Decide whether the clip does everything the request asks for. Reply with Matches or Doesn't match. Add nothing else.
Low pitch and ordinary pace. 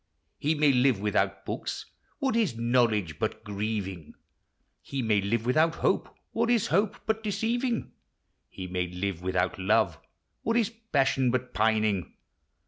Matches